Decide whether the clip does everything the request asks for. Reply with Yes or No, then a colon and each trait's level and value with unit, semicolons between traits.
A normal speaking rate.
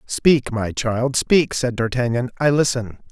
Yes: average, 155 wpm